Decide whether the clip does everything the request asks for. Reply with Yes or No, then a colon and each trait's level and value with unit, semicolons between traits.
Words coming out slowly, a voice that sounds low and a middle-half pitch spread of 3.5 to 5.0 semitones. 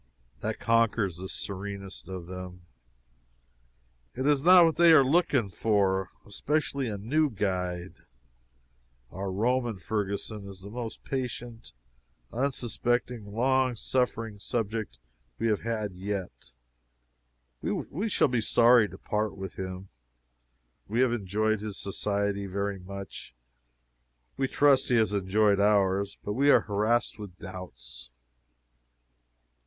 Yes: slow, 120 wpm; low, 105 Hz; average, 3.9 semitones